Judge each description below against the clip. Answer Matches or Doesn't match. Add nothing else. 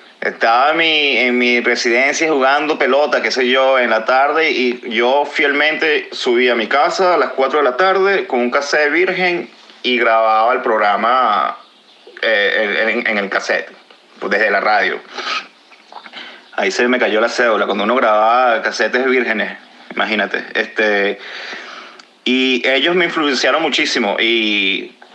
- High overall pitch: Doesn't match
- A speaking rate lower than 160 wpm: Matches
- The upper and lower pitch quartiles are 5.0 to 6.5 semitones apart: Doesn't match